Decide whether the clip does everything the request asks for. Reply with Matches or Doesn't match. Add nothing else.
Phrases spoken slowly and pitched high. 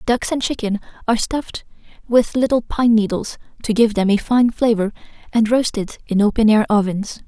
Doesn't match